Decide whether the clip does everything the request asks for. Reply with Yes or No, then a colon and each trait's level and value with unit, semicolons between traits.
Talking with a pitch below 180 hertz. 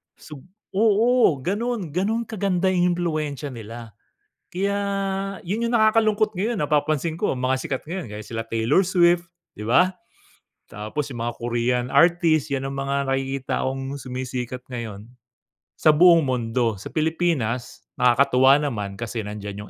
Yes: medium, 140 Hz